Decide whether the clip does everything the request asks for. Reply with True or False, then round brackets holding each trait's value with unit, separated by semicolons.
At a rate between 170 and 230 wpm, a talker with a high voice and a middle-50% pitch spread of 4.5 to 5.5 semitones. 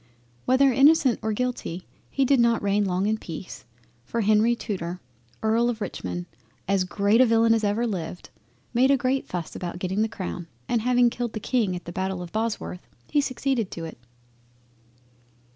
True (175 wpm; 220 Hz; 4.8 semitones)